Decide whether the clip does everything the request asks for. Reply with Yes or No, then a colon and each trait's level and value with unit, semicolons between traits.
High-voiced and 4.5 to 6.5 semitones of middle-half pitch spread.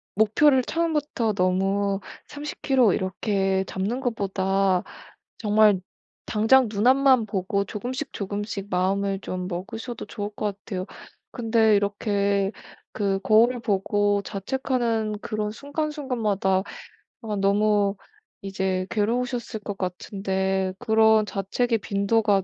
No: high, 205 Hz; average, 2.9 semitones